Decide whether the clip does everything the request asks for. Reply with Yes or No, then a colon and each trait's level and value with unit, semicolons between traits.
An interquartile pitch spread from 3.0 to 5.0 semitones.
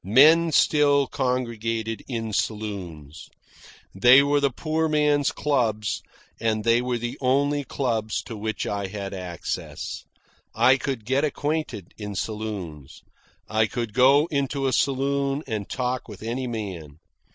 Yes: average, 4.7 semitones